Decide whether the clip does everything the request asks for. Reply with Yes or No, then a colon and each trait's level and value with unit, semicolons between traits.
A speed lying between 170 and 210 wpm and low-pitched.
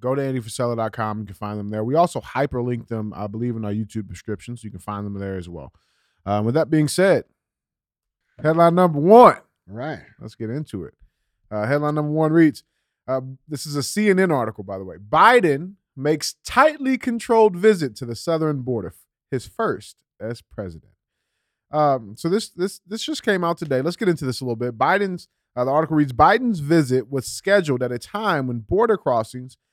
Yes: average, 200 wpm; low, 130 Hz